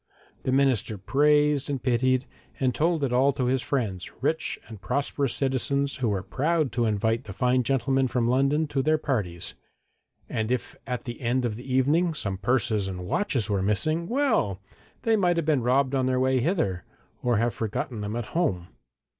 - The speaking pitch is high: No, low, 130 Hz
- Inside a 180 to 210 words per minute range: Yes, average, 185 wpm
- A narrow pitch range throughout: No, average, 4.0 semitones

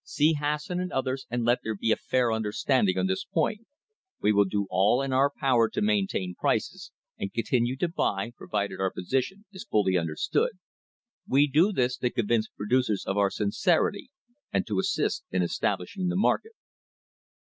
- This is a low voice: Yes, low, 120 Hz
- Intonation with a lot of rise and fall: Yes, wide, 6.7 semitones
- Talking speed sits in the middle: Yes, average, 175 wpm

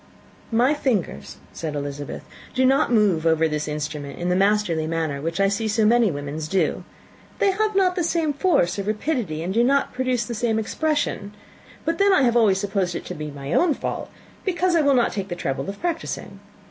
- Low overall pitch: No, high, 210 Hz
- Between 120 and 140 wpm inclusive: No, fast, 205 wpm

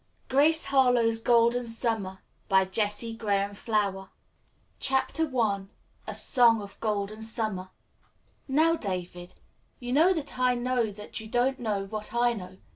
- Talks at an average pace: No, slow, 120 wpm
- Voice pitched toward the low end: No, high, 225 Hz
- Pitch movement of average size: Yes, average, 3.7 semitones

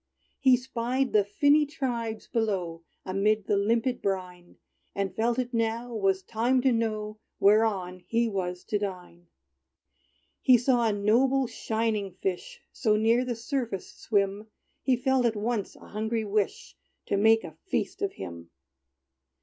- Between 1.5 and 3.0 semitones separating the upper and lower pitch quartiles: No, average, 3.5 semitones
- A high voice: Yes, high, 220 Hz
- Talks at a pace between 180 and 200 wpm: No, average, 145 wpm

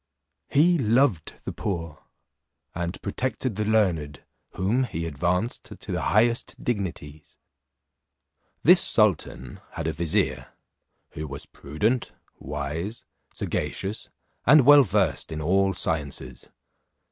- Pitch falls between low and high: No, very low, 95 Hz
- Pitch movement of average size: No, wide, 6.9 semitones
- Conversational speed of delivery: No, slow, 110 wpm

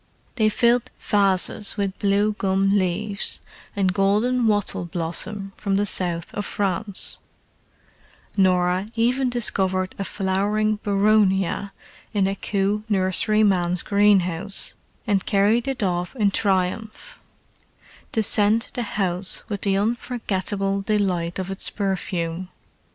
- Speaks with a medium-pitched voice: No, high, 200 Hz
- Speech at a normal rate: No, slow, 115 wpm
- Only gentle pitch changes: Yes, narrow, 2.2 semitones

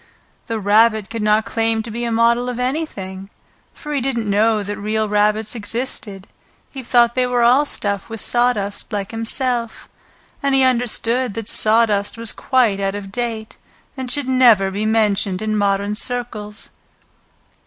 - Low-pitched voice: No, high, 225 Hz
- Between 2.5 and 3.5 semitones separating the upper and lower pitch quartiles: Yes, average, 2.9 semitones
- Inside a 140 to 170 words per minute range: Yes, average, 160 wpm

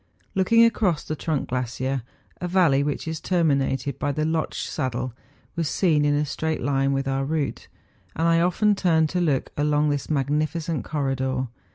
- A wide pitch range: No, average, 3.3 semitones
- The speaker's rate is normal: Yes, average, 170 wpm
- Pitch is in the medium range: Yes, medium, 150 Hz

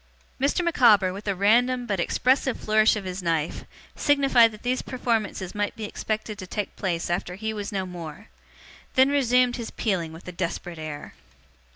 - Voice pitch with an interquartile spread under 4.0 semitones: No, average, 5.1 semitones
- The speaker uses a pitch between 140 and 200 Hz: No, high, 210 Hz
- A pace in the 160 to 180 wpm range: Yes, average, 175 wpm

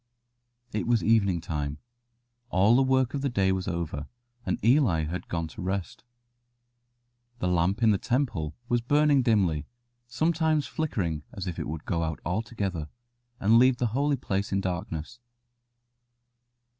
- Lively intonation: Yes, wide, 6.3 semitones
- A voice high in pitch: No, low, 100 Hz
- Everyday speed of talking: Yes, average, 150 wpm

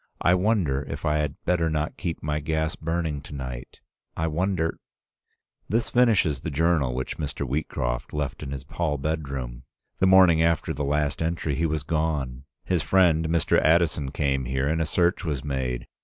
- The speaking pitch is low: Yes, very low, 75 Hz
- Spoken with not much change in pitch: No, average, 3.1 semitones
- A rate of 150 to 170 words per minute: No, average, 180 wpm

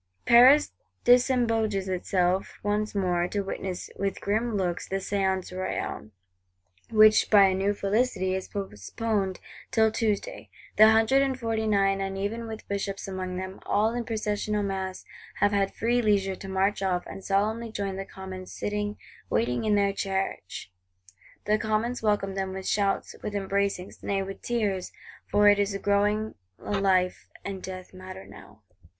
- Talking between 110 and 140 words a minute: No, average, 155 wpm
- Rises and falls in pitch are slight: Yes, narrow, 2.1 semitones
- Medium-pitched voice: No, high, 200 Hz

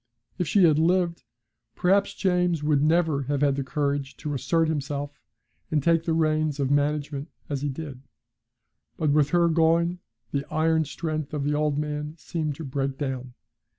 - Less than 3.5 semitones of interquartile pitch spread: Yes, narrow, 2.4 semitones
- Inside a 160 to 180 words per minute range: Yes, average, 170 wpm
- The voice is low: No, medium, 150 Hz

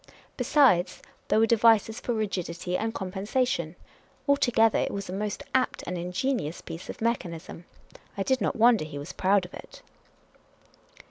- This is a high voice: Yes, high, 205 Hz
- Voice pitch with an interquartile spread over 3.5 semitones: Yes, average, 4.6 semitones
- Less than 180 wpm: Yes, average, 155 wpm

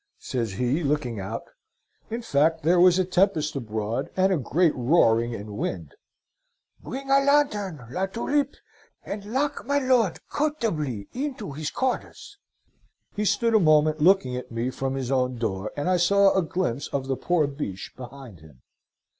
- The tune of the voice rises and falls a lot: Yes, wide, 8.0 semitones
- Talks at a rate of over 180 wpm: No, average, 165 wpm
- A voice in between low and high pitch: Yes, medium, 155 Hz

